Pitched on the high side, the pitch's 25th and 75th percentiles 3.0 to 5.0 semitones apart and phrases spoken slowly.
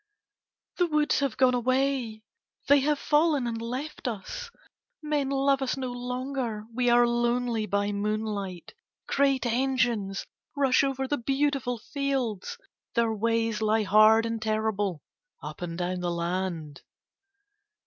Yes: high, 240 Hz; average, 4.2 semitones; slow, 130 wpm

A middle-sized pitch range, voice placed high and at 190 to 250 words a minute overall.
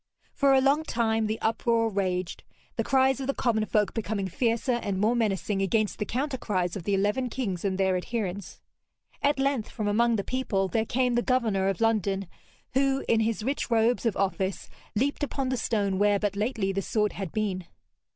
Yes: average, 4.0 semitones; high, 220 Hz; average, 195 wpm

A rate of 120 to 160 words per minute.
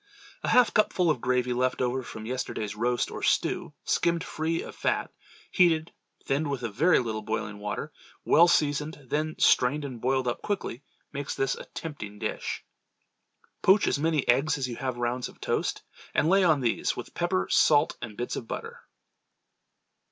No: average, 175 wpm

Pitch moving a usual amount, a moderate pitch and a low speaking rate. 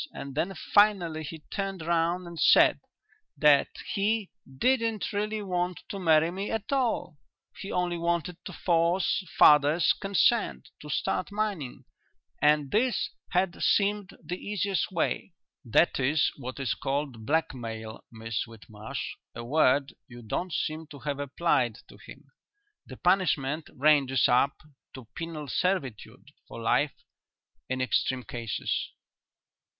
No: wide, 5.9 semitones; medium, 160 Hz; slow, 130 wpm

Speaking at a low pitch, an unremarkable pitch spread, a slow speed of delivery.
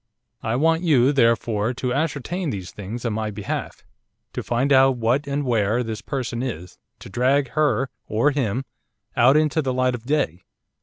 No: low, 125 Hz; average, 3.7 semitones; average, 170 wpm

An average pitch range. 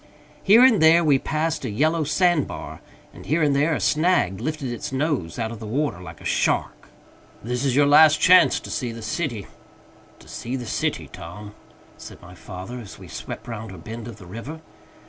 No: wide, 6.2 semitones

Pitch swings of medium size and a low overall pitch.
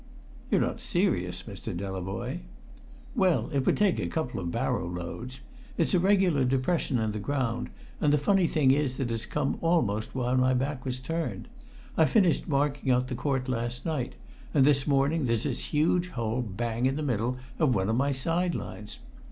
Yes: average, 4.4 semitones; low, 130 Hz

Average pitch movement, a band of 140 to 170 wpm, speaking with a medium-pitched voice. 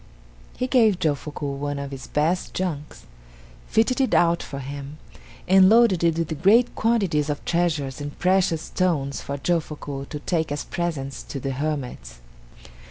Yes: average, 4.5 semitones; average, 155 wpm; medium, 155 Hz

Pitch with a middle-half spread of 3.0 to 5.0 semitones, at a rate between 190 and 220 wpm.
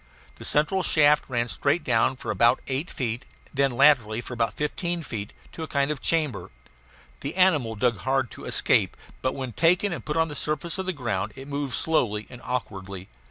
Yes: average, 4.4 semitones; average, 200 wpm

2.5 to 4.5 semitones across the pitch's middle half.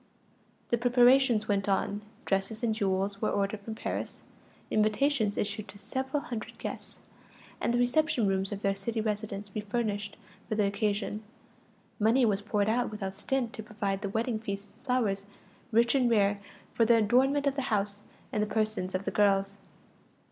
Yes: average, 2.9 semitones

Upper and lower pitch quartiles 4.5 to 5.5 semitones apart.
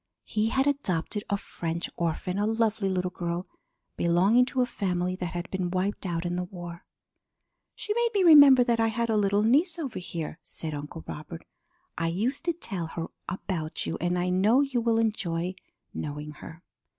Yes: average, 5.1 semitones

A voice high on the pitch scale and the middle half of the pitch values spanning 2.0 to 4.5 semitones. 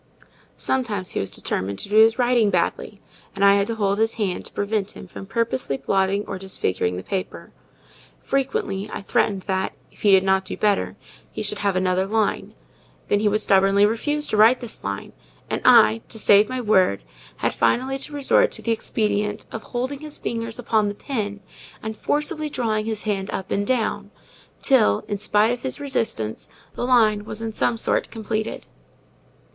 Yes: high, 210 Hz; average, 2.8 semitones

